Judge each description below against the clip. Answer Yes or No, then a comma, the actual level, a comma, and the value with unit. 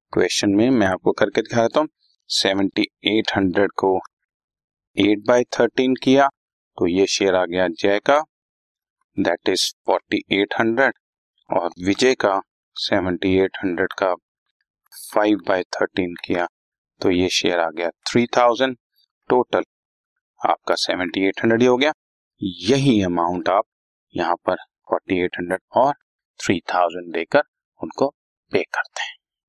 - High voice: No, low, 105 Hz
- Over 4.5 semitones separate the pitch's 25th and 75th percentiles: Yes, wide, 5.5 semitones